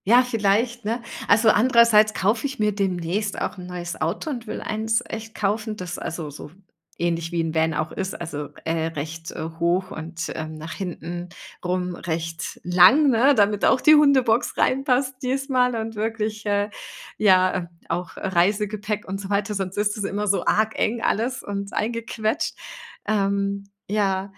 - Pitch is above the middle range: Yes, high, 205 Hz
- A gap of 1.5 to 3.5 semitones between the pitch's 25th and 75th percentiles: No, average, 4.1 semitones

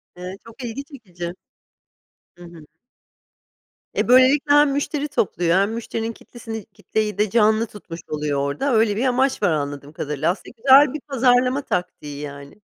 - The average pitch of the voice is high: Yes, high, 220 Hz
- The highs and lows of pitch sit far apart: Yes, wide, 7.1 semitones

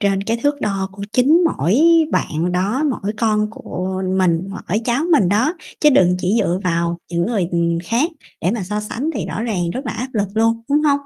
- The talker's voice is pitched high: Yes, high, 205 Hz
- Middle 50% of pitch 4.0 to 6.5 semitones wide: Yes, average, 4.8 semitones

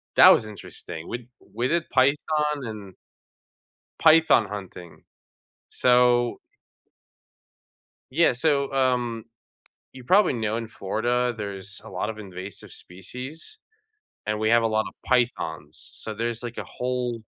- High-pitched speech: No, low, 120 Hz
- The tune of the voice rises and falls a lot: No, average, 3.4 semitones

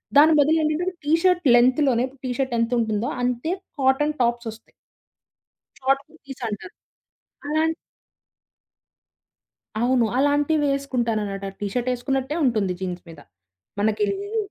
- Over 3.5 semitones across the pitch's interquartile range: Yes, average, 4.5 semitones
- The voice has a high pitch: Yes, very high, 260 Hz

